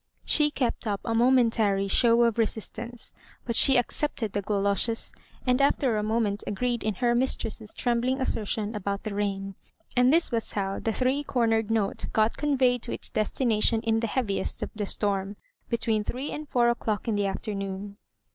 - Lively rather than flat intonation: No, average, 3.1 semitones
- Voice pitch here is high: Yes, high, 225 Hz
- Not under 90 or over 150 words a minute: No, average, 175 wpm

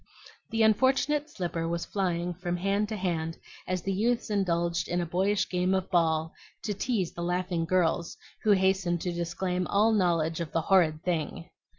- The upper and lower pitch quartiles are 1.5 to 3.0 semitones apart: Yes, narrow, 2.6 semitones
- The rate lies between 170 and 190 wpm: Yes, average, 175 wpm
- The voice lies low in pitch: No, medium, 180 Hz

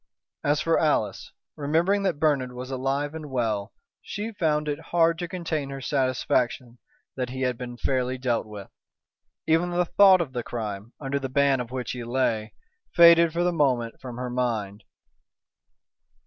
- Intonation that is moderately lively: Yes, average, 4.7 semitones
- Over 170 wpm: No, average, 165 wpm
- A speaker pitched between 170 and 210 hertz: No, low, 135 Hz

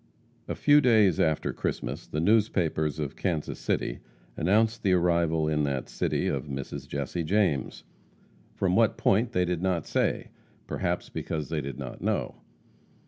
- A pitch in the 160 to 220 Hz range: No, very low, 85 Hz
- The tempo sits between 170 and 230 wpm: No, average, 150 wpm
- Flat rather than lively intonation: No, average, 4.7 semitones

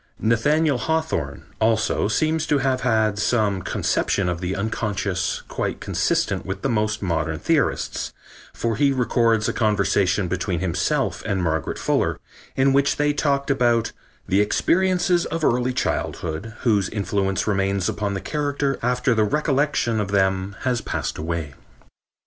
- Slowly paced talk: No, average, 145 wpm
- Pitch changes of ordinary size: No, wide, 5.8 semitones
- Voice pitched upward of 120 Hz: No, low, 110 Hz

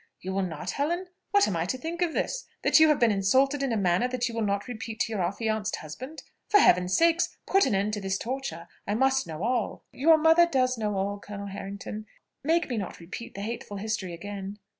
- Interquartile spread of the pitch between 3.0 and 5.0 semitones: No, wide, 5.6 semitones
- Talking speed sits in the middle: No, fast, 225 wpm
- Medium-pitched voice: No, high, 220 Hz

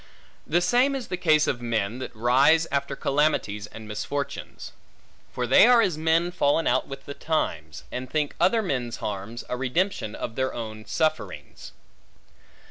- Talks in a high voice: No, medium, 140 Hz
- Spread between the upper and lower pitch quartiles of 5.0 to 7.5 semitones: Yes, wide, 5.6 semitones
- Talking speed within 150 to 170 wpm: Yes, average, 160 wpm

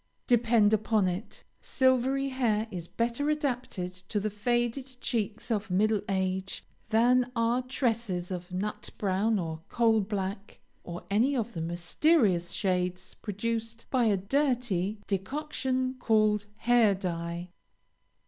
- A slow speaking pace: Yes, slow, 125 wpm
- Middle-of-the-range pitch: No, high, 215 Hz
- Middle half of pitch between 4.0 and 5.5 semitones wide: Yes, average, 4.3 semitones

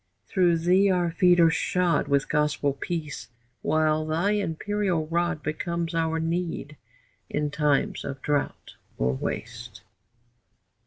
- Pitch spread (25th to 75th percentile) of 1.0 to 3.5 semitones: Yes, average, 2.8 semitones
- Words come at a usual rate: No, slow, 120 wpm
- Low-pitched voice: No, medium, 165 Hz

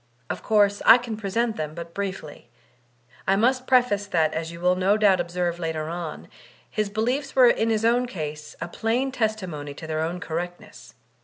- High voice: Yes, high, 195 Hz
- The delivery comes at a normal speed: Yes, average, 185 wpm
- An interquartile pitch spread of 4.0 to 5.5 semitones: Yes, average, 5.1 semitones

